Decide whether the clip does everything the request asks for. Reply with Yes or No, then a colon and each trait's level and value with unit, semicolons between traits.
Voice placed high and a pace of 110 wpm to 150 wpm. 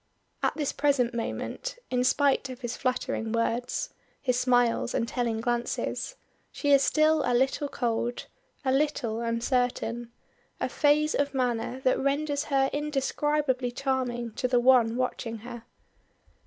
Yes: very high, 255 Hz; average, 140 wpm